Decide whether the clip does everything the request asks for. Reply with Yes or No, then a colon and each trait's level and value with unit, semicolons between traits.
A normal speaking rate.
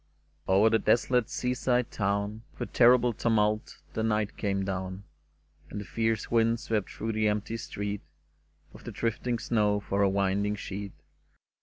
Yes: average, 160 wpm